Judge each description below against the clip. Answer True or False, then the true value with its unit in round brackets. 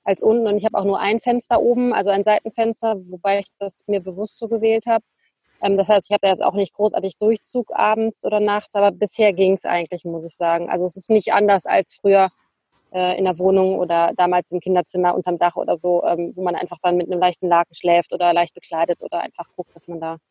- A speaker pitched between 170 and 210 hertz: True (190 Hz)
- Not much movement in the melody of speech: False (3.0 semitones)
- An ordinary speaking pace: False (240 wpm)